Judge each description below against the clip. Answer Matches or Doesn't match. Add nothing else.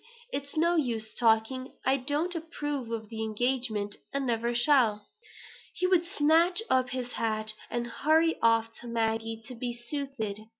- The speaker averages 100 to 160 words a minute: Matches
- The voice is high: Matches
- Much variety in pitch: Doesn't match